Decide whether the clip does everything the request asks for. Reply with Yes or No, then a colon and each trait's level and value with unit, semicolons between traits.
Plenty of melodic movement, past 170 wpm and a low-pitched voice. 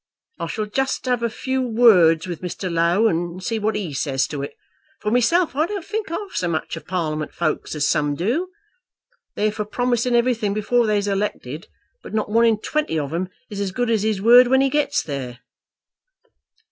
No: wide, 6.4 semitones; average, 195 wpm; high, 210 Hz